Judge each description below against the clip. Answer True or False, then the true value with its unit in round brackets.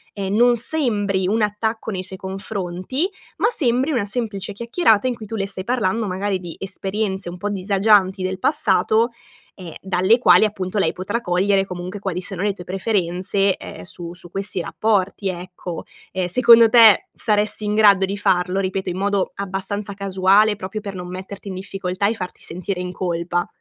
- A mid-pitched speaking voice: False (195 Hz)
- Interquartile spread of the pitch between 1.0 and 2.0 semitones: False (2.4 semitones)